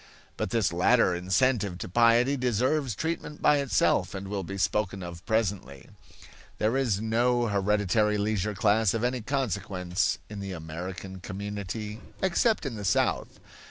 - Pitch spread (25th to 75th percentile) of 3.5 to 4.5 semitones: Yes, average, 4.1 semitones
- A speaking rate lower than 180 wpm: Yes, average, 145 wpm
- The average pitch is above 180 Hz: No, low, 105 Hz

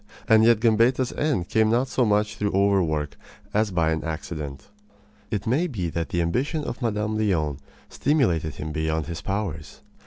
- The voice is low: Yes, low, 100 Hz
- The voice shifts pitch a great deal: Yes, wide, 5.9 semitones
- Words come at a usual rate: Yes, average, 165 wpm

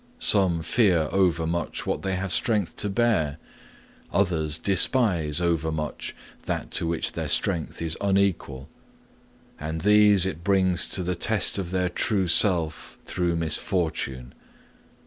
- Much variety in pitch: No, average, 3.4 semitones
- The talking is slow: Yes, slow, 125 wpm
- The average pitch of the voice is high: No, very low, 90 Hz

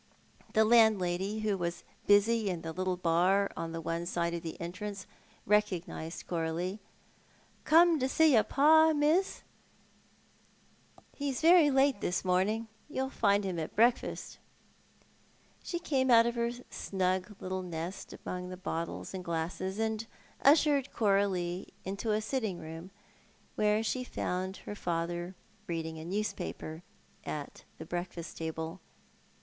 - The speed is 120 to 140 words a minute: Yes, slow, 135 wpm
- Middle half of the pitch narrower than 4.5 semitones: No, average, 4.8 semitones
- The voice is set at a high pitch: Yes, high, 195 Hz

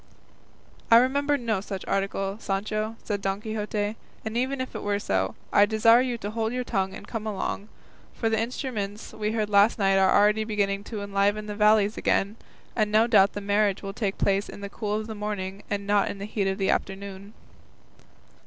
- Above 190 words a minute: Yes, average, 200 wpm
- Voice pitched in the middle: No, high, 210 Hz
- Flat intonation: Yes, narrow, 1.8 semitones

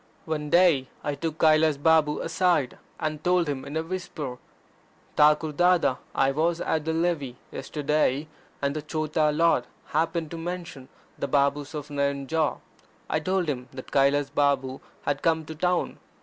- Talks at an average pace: Yes, average, 155 wpm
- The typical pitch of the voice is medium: Yes, medium, 150 Hz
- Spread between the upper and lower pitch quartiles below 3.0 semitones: Yes, narrow, 2.5 semitones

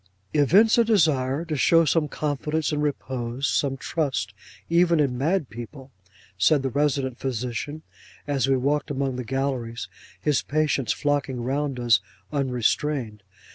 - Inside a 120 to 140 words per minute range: Yes, slow, 135 wpm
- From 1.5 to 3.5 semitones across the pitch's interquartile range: Yes, average, 2.9 semitones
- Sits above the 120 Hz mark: Yes, medium, 140 Hz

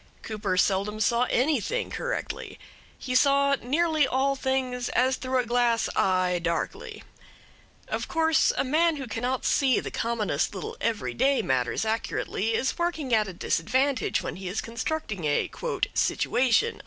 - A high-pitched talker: Yes, high, 245 Hz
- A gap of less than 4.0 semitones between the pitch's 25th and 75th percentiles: No, average, 4.6 semitones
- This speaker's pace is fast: No, average, 145 wpm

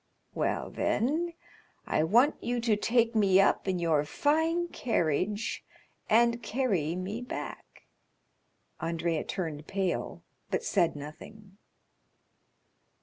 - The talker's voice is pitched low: No, high, 205 Hz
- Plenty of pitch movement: Yes, wide, 5.9 semitones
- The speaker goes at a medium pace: No, slow, 105 wpm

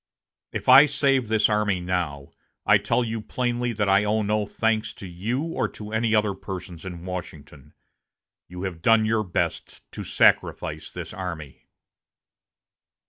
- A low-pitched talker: Yes, low, 105 Hz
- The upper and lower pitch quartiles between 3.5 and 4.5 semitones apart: Yes, average, 3.8 semitones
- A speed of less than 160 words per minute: Yes, average, 150 wpm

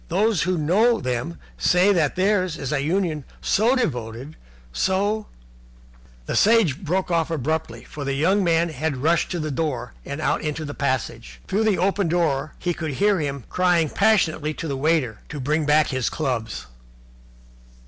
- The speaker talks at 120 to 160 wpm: No, average, 170 wpm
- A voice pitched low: No, medium, 155 Hz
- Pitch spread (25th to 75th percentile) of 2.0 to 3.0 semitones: No, average, 5.0 semitones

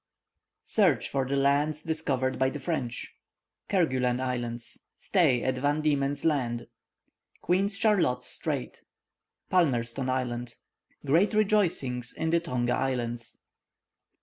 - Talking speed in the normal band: No, slow, 110 wpm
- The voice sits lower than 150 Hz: Yes, low, 135 Hz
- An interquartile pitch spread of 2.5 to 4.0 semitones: No, average, 4.6 semitones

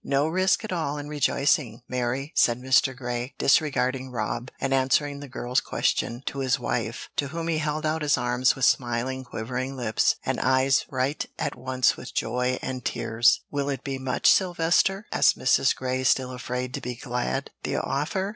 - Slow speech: No, average, 180 wpm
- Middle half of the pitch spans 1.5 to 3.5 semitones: Yes, narrow, 2.6 semitones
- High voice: No, low, 130 Hz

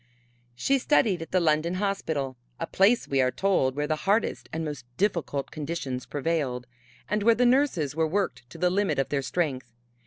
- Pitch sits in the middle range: Yes, medium, 165 Hz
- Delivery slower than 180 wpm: No, average, 185 wpm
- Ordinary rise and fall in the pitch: No, wide, 6.1 semitones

